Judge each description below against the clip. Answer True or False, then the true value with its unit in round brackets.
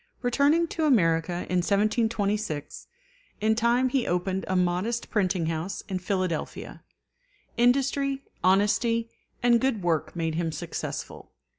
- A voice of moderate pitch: False (205 Hz)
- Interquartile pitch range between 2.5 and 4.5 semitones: False (5.3 semitones)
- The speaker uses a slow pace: True (120 wpm)